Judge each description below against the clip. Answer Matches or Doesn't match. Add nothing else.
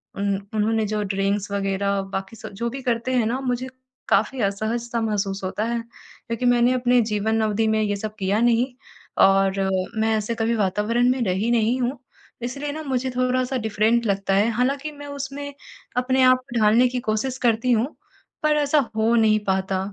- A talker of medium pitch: Doesn't match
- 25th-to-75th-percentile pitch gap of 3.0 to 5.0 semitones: Matches